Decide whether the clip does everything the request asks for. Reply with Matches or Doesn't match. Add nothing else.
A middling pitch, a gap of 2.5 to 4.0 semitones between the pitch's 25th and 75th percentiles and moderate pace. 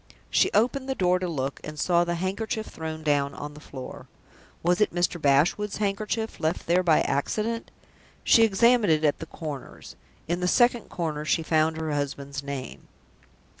Doesn't match